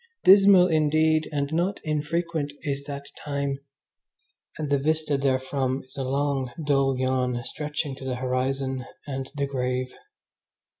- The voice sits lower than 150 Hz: Yes, medium, 140 Hz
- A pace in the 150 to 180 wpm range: No, slow, 135 wpm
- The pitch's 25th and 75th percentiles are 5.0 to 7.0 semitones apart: No, narrow, 2.6 semitones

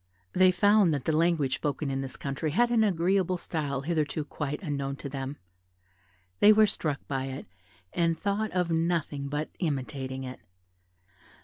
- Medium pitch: Yes, medium, 155 Hz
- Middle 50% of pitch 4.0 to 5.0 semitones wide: Yes, average, 4.5 semitones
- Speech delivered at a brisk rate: No, average, 155 wpm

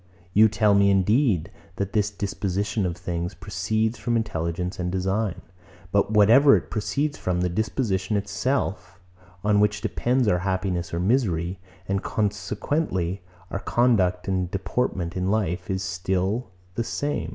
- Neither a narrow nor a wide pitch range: Yes, average, 3.2 semitones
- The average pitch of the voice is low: Yes, low, 100 Hz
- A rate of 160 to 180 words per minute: No, average, 140 wpm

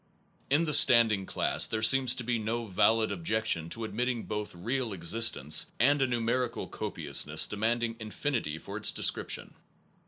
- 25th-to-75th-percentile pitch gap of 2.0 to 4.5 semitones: Yes, narrow, 2.6 semitones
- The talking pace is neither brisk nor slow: Yes, average, 180 wpm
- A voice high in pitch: No, low, 115 Hz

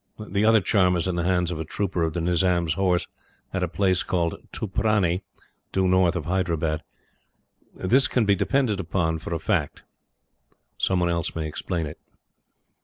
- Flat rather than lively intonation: Yes, narrow, 2.3 semitones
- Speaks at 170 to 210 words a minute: Yes, average, 175 wpm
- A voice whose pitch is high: No, very low, 90 Hz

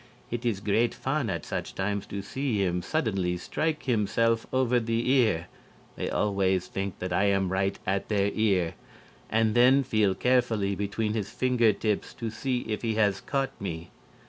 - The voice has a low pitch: Yes, low, 105 Hz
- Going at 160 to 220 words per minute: Yes, average, 170 wpm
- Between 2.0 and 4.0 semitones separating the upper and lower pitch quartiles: Yes, average, 3.6 semitones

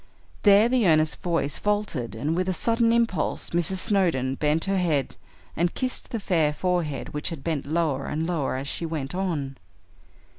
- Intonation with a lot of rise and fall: No, average, 4.5 semitones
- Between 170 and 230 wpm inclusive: Yes, average, 175 wpm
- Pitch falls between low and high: Yes, medium, 165 Hz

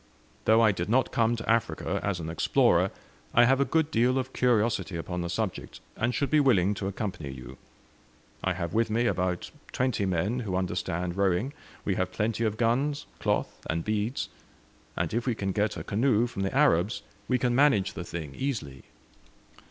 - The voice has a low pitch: Yes, low, 110 Hz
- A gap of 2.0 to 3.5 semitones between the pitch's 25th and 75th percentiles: No, average, 4.9 semitones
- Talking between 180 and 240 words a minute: Yes, average, 185 wpm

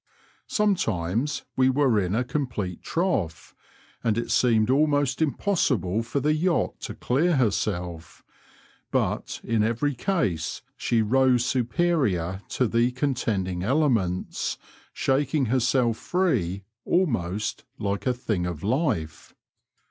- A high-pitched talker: No, low, 120 Hz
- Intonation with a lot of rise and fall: Yes, wide, 6.5 semitones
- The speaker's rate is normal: No, slow, 115 wpm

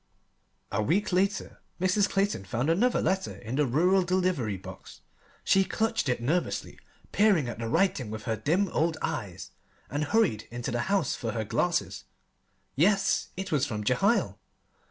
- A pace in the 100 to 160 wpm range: Yes, average, 155 wpm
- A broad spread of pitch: Yes, wide, 8.5 semitones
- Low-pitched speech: No, medium, 160 Hz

